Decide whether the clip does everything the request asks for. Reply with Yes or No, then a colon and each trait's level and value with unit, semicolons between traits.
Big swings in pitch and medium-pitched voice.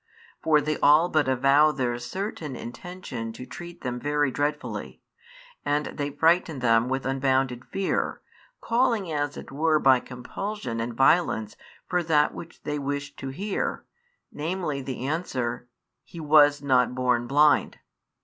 No: average, 3.8 semitones; medium, 145 Hz